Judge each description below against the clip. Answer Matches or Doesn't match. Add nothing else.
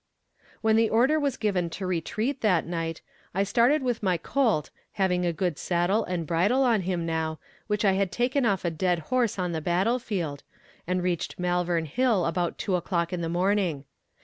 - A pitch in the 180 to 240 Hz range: Matches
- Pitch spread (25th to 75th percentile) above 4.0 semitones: Matches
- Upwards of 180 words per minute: Matches